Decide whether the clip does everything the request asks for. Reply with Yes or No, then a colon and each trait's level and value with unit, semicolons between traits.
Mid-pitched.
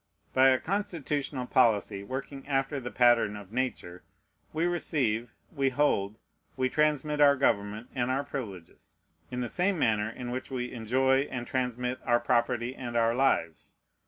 No: low, 125 Hz